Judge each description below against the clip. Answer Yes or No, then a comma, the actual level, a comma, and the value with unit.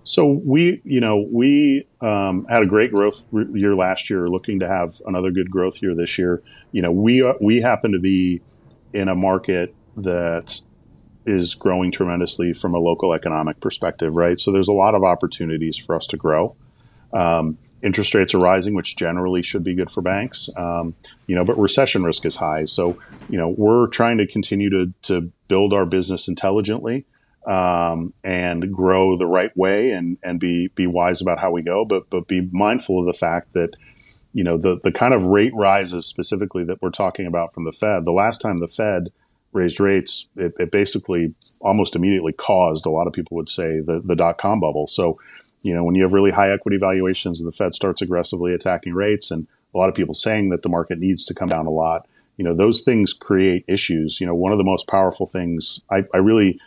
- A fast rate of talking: Yes, fast, 210 wpm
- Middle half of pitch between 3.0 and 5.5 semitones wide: No, narrow, 2.6 semitones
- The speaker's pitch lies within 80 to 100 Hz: Yes, very low, 95 Hz